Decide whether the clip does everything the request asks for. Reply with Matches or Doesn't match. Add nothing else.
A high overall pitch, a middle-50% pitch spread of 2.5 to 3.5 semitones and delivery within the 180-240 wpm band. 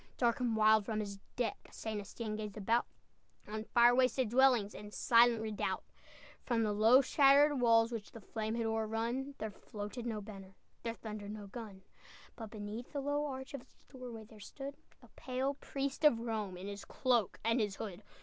Matches